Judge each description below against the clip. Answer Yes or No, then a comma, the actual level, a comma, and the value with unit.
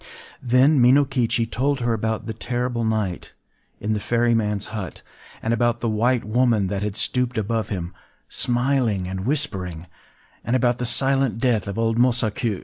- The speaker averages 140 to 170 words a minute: Yes, average, 150 wpm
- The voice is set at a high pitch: No, low, 115 Hz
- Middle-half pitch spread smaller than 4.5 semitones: Yes, average, 2.9 semitones